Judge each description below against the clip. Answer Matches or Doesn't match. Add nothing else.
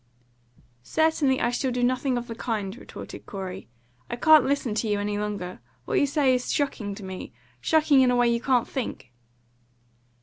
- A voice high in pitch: Matches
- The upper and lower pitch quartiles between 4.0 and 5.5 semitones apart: Matches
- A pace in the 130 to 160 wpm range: Doesn't match